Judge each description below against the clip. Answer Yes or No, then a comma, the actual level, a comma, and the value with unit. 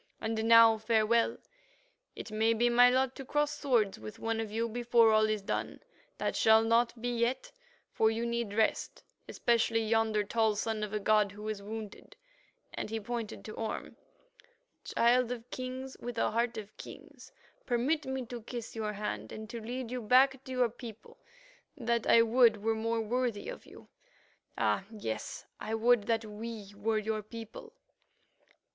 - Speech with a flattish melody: Yes, narrow, 1.9 semitones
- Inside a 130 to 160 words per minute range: No, average, 170 wpm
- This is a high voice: Yes, high, 225 Hz